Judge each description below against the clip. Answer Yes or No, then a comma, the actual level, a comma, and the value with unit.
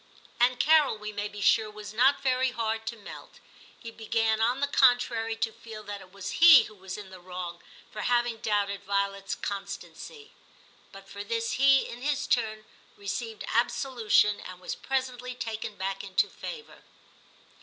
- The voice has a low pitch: No, high, 220 Hz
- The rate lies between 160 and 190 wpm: Yes, average, 165 wpm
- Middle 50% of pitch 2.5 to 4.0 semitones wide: Yes, average, 3.5 semitones